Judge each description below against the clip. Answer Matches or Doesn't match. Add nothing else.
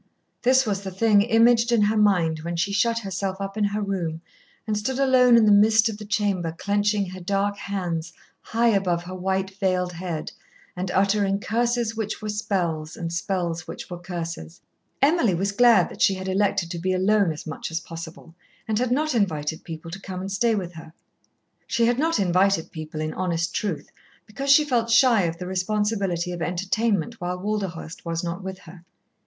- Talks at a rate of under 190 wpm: Doesn't match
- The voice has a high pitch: Matches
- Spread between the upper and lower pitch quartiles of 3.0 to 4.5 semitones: Matches